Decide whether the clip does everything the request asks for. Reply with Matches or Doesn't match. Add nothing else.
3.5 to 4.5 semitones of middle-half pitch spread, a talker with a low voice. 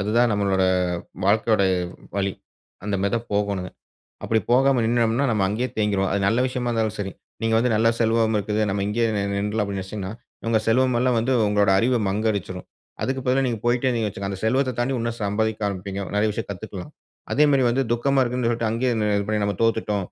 Doesn't match